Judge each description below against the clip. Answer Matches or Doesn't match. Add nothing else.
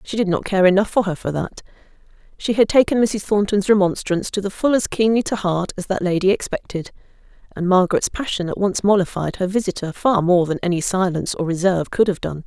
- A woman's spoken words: Matches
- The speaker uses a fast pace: Matches